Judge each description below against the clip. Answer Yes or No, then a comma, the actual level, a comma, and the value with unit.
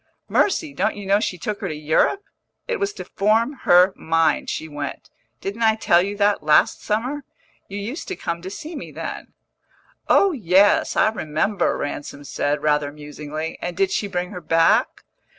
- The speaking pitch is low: No, high, 190 Hz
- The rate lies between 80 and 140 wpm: No, average, 180 wpm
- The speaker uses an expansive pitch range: Yes, wide, 5.7 semitones